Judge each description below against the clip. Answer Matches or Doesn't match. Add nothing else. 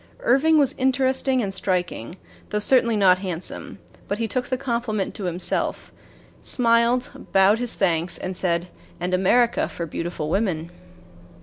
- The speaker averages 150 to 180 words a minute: Doesn't match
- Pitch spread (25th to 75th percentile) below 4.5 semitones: Doesn't match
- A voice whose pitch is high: Matches